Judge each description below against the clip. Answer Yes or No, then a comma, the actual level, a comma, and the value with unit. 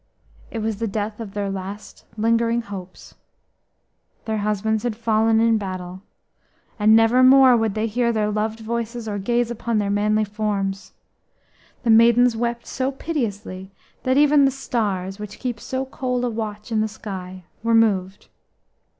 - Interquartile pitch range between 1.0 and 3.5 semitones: Yes, narrow, 2.4 semitones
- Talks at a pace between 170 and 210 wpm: No, average, 160 wpm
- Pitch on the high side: Yes, high, 220 Hz